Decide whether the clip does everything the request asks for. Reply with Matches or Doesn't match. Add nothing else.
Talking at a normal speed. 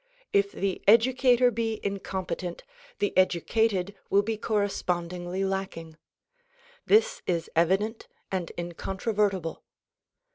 Doesn't match